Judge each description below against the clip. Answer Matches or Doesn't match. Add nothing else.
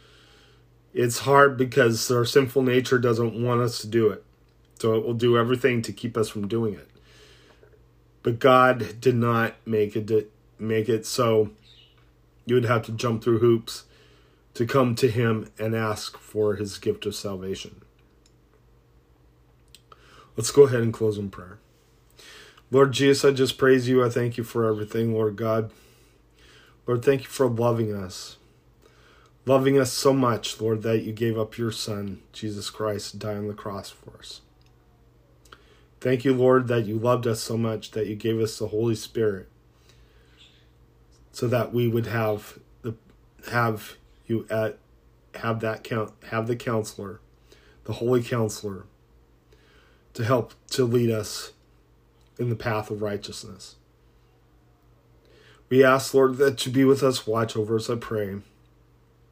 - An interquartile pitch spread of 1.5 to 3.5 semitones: Matches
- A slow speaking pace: Doesn't match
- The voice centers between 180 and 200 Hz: Doesn't match